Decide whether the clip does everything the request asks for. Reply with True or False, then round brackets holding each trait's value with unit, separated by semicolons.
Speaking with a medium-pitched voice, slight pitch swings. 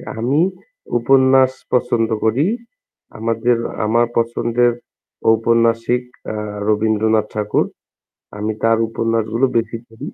False (115 Hz; 1.7 semitones)